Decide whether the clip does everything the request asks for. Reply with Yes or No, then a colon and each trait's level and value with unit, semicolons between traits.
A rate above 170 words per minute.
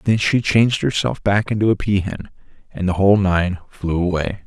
Yes: average, 200 wpm